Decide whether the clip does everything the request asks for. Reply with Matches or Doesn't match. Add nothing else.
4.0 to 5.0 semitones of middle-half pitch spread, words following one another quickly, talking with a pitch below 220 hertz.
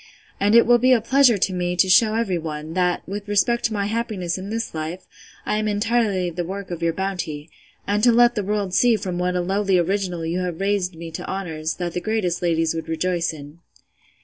Doesn't match